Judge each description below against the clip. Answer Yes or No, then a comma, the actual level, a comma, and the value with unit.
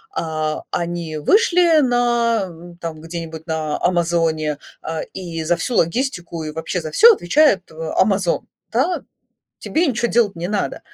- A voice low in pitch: No, medium, 175 Hz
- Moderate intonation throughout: No, wide, 6.6 semitones